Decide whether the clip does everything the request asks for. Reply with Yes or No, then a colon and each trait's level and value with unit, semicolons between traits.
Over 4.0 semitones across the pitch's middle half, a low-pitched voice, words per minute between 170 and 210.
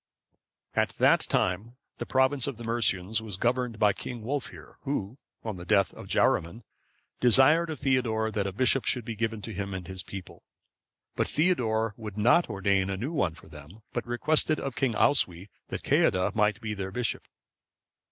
Yes: average, 4.4 semitones; low, 110 Hz; average, 180 wpm